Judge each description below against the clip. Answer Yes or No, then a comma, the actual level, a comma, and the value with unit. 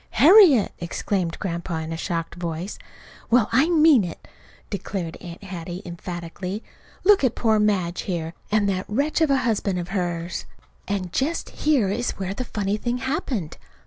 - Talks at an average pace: Yes, average, 160 wpm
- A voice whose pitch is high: Yes, high, 195 Hz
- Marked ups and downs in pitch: Yes, wide, 5.9 semitones